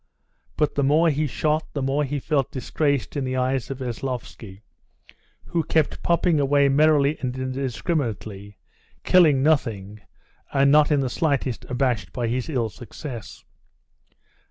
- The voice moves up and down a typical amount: Yes, average, 3.3 semitones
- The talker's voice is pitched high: No, low, 135 Hz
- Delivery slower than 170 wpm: Yes, average, 140 wpm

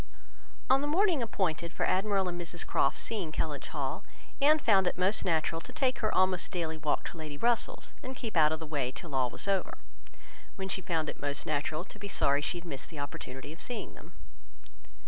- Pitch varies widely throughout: No, average, 5.0 semitones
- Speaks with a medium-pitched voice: Yes, medium, 175 Hz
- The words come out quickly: Yes, fast, 215 wpm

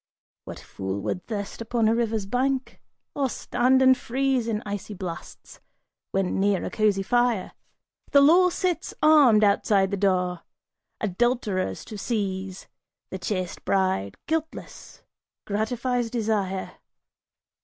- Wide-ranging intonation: No, average, 4.4 semitones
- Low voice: No, high, 215 Hz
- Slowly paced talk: Yes, slow, 120 wpm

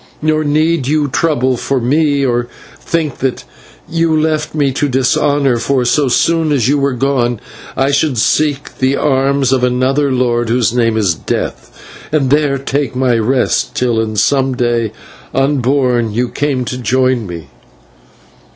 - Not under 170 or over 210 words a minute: No, average, 155 wpm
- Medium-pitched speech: No, low, 130 Hz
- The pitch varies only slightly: No, average, 3.0 semitones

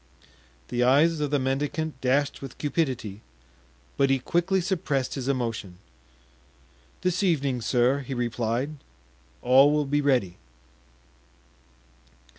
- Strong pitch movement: No, average, 3.2 semitones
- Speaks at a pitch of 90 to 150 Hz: Yes, low, 135 Hz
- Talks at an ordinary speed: No, slow, 110 wpm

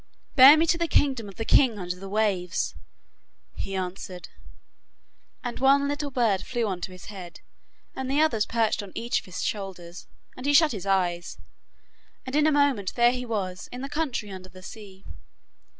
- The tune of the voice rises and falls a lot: Yes, wide, 6.1 semitones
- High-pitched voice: Yes, high, 220 Hz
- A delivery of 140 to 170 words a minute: No, average, 185 wpm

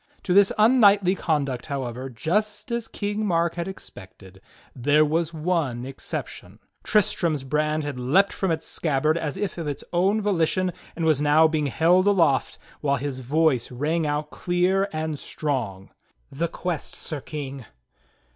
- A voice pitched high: No, medium, 155 Hz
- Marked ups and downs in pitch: No, average, 4.6 semitones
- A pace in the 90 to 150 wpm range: No, average, 160 wpm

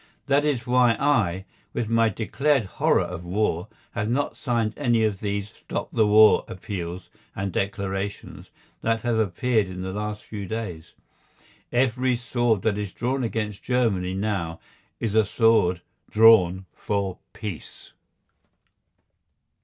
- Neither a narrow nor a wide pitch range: Yes, average, 3.4 semitones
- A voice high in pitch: No, low, 105 Hz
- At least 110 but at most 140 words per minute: Yes, slow, 135 wpm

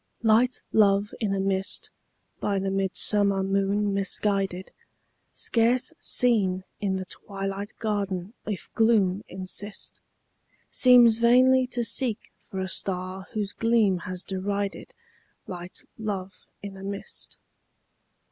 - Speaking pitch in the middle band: No, high, 200 Hz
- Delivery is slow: Yes, slow, 115 wpm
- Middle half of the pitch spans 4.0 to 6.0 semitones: No, narrow, 2.4 semitones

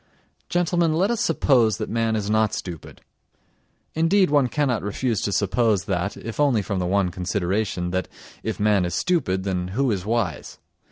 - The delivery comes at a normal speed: Yes, average, 170 wpm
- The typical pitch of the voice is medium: No, low, 110 Hz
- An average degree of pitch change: No, wide, 6.4 semitones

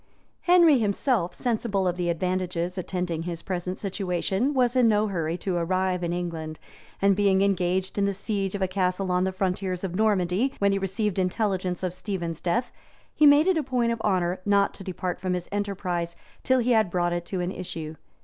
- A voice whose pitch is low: No, high, 190 Hz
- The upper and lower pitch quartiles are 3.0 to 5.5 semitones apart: No, narrow, 2.6 semitones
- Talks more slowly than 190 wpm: No, average, 195 wpm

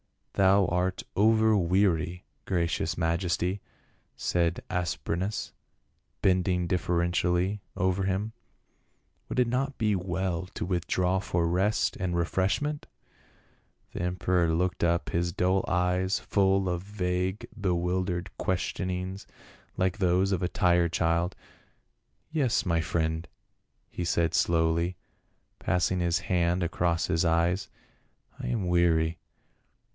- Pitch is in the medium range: No, very low, 90 Hz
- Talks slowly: Yes, slow, 120 wpm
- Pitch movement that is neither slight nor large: No, narrow, 1.7 semitones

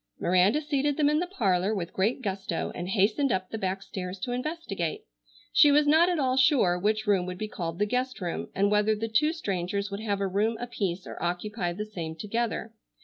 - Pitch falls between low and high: No, high, 210 Hz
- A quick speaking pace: Yes, fast, 210 wpm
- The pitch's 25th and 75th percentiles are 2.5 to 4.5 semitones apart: No, wide, 5.5 semitones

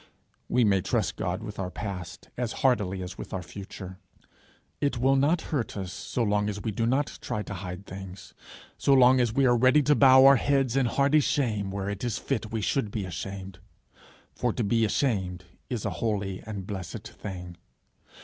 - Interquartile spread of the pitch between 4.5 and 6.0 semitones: Yes, average, 5.0 semitones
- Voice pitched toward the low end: Yes, low, 105 Hz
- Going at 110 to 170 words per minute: No, average, 195 wpm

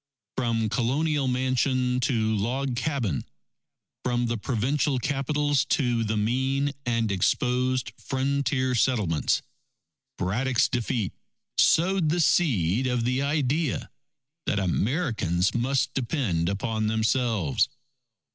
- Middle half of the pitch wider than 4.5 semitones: No, average, 3.7 semitones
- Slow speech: Yes, slow, 100 wpm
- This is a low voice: Yes, low, 125 Hz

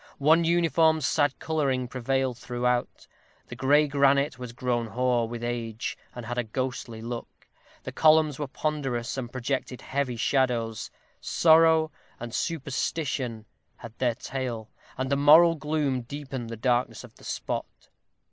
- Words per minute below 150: Yes, average, 140 wpm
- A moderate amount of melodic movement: Yes, average, 3.4 semitones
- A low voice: Yes, low, 130 Hz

